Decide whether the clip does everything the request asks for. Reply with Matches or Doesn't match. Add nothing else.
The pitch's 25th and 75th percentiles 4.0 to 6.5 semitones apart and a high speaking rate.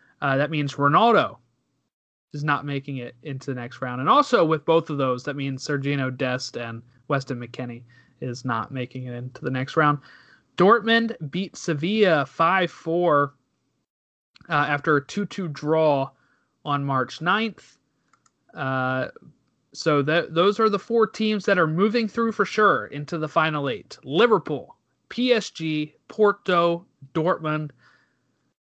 Doesn't match